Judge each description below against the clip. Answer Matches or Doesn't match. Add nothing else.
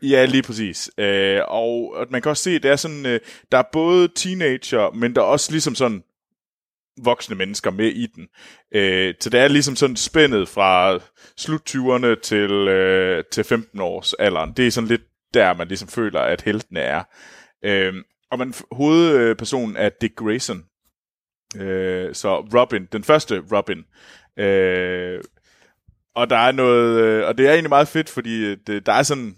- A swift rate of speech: Doesn't match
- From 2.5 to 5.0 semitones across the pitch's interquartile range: Doesn't match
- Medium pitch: Doesn't match